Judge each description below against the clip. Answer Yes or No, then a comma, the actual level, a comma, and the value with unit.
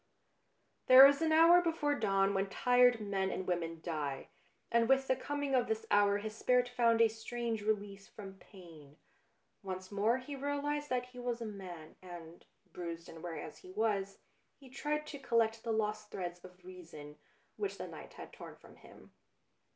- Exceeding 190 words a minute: No, average, 180 wpm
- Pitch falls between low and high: No, high, 215 Hz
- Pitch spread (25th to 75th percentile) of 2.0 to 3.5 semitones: No, average, 5.2 semitones